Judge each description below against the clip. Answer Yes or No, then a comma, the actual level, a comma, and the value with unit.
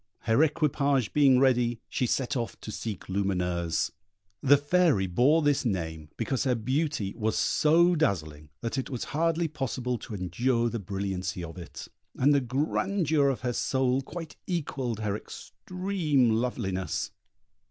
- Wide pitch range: Yes, wide, 6.4 semitones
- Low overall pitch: Yes, low, 125 Hz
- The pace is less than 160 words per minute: Yes, average, 145 wpm